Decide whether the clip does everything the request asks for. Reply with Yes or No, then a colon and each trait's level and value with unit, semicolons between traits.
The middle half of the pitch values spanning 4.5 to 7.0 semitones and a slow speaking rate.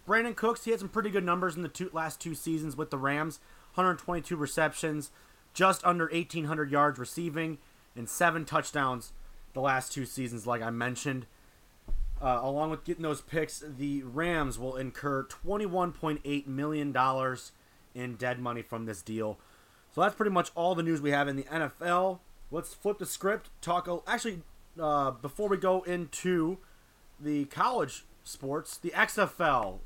No: average, 5.0 semitones; average, 165 wpm